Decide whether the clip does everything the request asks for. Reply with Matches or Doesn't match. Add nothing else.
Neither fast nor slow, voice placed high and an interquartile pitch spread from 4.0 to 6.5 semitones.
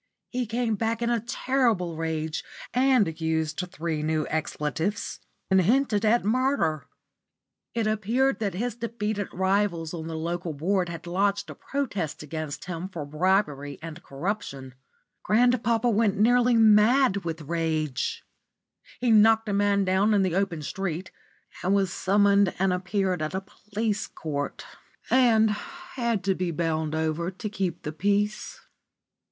Matches